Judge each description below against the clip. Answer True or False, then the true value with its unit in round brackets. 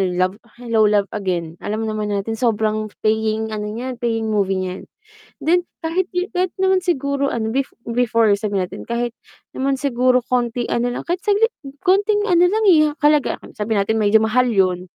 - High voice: True (230 Hz)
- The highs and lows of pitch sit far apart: True (5.8 semitones)